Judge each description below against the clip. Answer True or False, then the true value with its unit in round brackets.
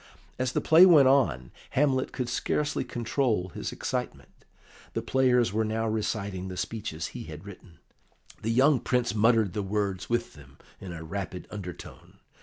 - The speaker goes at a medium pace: True (160 wpm)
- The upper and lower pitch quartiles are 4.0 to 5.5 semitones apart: True (5.2 semitones)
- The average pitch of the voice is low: True (110 Hz)